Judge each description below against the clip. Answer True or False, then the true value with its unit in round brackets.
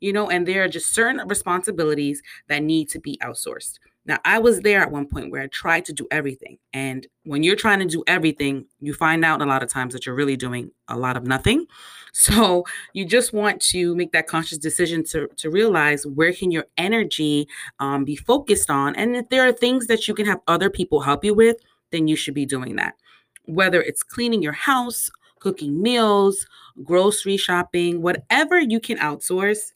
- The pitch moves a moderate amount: False (6.2 semitones)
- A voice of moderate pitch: True (175 Hz)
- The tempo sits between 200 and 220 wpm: True (205 wpm)